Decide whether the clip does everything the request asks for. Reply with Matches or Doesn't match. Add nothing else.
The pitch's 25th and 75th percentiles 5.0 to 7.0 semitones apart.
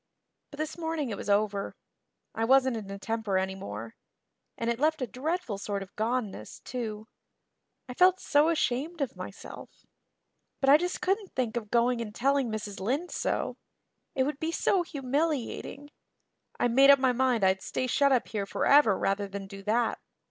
Matches